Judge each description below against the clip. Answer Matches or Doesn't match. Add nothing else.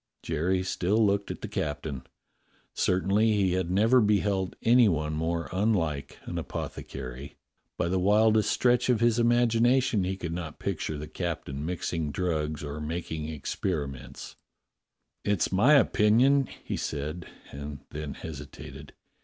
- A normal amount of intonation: Doesn't match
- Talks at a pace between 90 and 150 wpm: Matches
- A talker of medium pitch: Doesn't match